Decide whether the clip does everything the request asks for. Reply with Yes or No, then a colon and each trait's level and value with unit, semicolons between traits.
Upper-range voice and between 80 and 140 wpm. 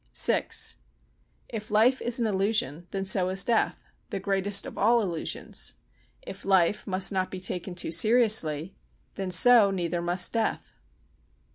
Yes: high, 195 Hz; slow, 135 wpm